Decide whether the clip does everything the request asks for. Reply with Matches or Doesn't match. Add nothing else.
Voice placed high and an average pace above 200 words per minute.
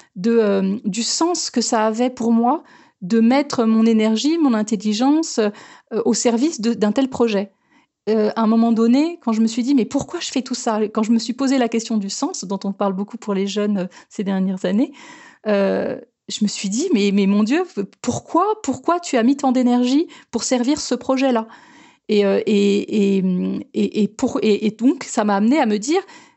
Matches